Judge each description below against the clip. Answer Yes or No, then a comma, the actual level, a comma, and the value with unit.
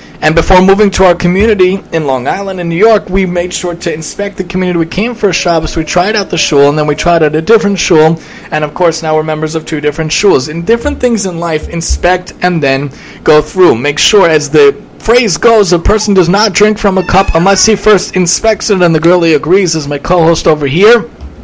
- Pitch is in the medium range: Yes, medium, 180 Hz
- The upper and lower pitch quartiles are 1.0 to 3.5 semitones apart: No, average, 4.0 semitones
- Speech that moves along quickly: Yes, fast, 240 wpm